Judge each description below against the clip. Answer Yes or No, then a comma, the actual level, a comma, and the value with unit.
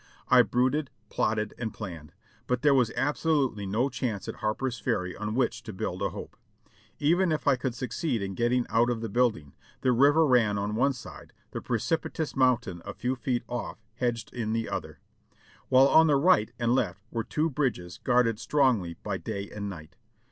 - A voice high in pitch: No, low, 120 Hz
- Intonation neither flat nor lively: Yes, average, 3.9 semitones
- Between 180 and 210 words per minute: Yes, average, 190 wpm